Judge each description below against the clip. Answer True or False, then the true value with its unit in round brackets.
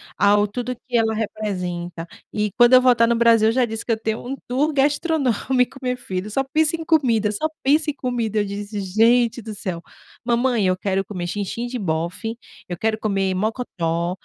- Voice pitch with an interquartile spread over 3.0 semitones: True (3.9 semitones)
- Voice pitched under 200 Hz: False (225 Hz)